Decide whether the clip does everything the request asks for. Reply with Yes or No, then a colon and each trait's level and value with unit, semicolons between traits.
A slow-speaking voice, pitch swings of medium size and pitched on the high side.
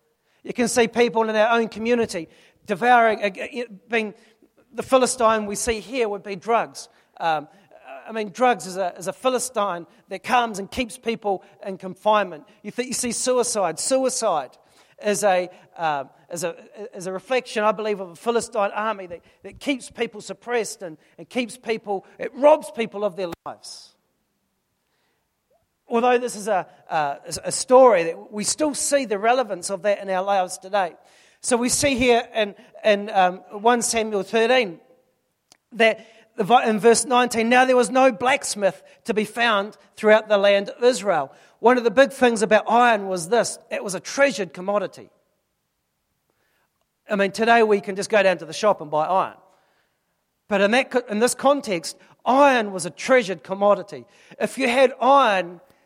No: average, 165 wpm; average, 3.6 semitones; high, 220 Hz